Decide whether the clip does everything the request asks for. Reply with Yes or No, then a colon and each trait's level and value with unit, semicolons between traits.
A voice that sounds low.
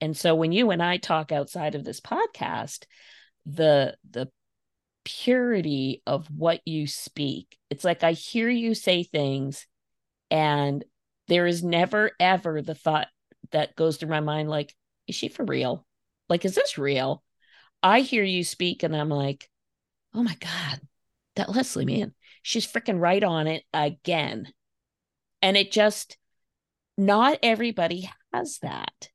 No: medium, 165 Hz